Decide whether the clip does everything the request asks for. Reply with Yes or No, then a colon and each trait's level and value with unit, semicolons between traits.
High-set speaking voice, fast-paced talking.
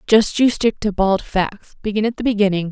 Yes: high, 205 Hz; fast, 220 wpm